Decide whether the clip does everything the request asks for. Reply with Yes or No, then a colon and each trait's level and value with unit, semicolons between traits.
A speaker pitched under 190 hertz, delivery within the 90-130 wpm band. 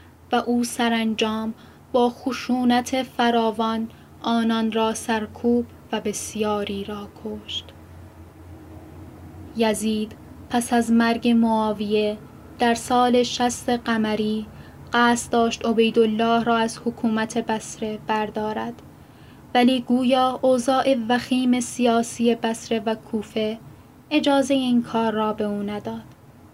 No: high, 230 Hz; slow, 105 wpm